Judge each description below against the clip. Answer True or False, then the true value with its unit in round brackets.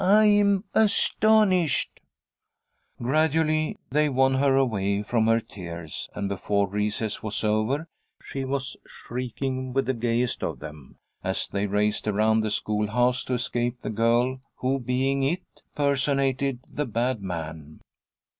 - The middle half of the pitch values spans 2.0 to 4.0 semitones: False (4.5 semitones)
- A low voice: True (125 Hz)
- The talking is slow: True (130 wpm)